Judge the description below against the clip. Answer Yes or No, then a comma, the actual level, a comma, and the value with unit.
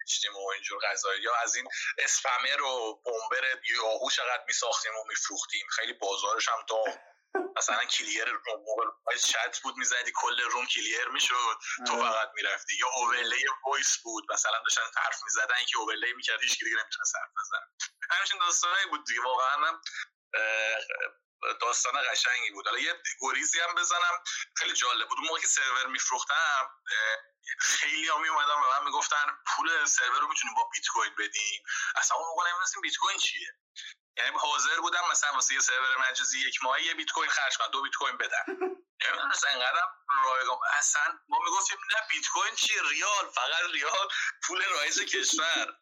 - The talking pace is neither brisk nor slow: No, fast, 165 wpm